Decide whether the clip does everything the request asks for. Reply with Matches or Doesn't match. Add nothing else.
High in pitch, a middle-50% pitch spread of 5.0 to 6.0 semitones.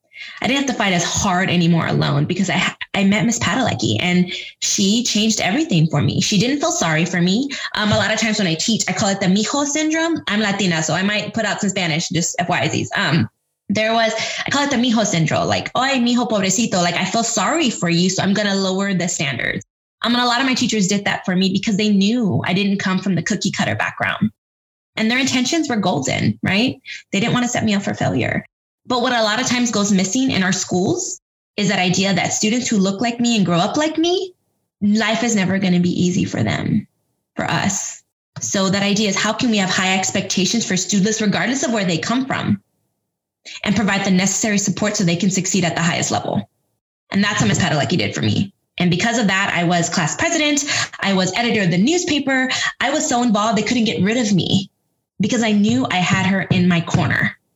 Doesn't match